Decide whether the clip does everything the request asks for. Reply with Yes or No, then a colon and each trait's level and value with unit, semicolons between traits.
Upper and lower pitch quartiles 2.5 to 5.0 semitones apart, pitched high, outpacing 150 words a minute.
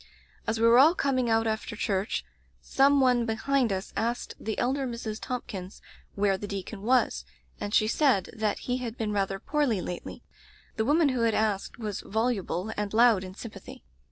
Yes: average, 3.5 semitones; high, 225 Hz; average, 180 wpm